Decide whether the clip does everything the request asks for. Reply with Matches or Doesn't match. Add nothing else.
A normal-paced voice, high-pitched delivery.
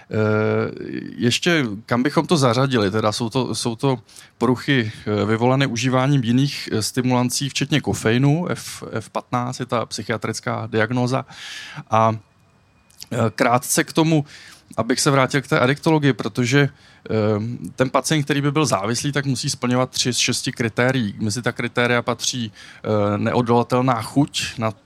Doesn't match